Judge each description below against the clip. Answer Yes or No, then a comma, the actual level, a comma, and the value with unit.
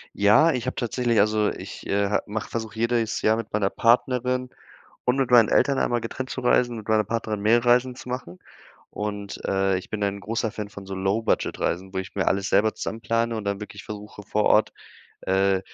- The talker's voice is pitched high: No, low, 110 Hz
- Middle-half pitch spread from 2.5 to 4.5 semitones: Yes, average, 2.9 semitones